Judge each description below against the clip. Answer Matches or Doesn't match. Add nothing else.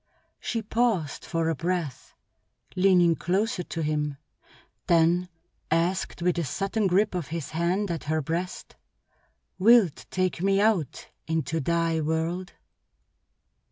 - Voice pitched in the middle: Matches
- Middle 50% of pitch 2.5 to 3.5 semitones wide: Matches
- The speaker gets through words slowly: Matches